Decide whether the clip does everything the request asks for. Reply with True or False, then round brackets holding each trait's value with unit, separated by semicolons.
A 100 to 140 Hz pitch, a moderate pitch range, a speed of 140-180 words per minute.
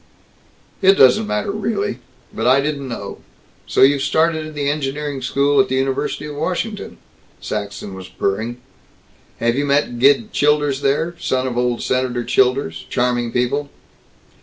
True (135 Hz; 3.3 semitones; 150 wpm)